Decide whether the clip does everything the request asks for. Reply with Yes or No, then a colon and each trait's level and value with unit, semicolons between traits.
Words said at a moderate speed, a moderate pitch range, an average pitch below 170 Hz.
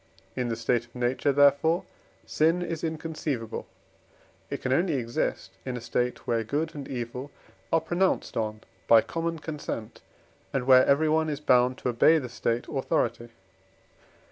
Yes: average, 150 wpm; average, 4.7 semitones; low, 135 Hz